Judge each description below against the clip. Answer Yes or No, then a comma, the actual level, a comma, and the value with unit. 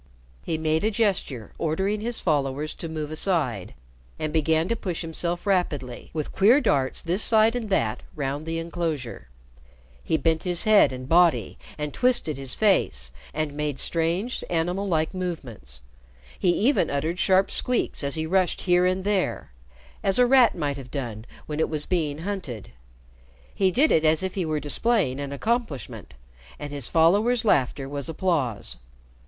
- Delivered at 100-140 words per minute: No, average, 165 wpm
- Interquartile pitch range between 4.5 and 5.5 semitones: Yes, average, 5.1 semitones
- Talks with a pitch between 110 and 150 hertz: No, medium, 160 Hz